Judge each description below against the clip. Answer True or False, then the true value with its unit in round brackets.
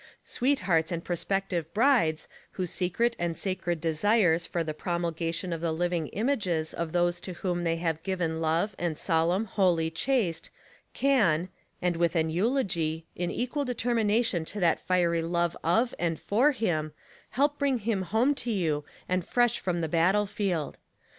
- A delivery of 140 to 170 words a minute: True (160 wpm)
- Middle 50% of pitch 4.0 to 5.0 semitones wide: True (4.3 semitones)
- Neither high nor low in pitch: True (175 Hz)